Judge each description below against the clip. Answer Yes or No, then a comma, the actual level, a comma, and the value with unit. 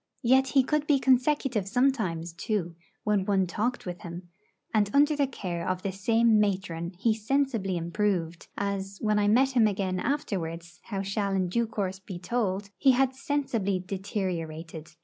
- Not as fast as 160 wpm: No, average, 165 wpm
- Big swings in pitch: No, average, 4.7 semitones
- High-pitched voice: Yes, high, 200 Hz